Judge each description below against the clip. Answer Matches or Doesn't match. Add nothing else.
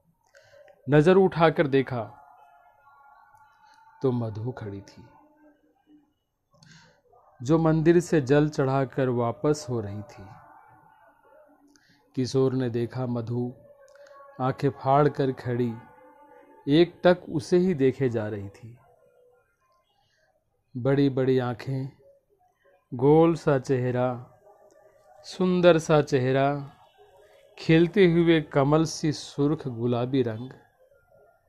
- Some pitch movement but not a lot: Doesn't match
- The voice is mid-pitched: Matches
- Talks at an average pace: Doesn't match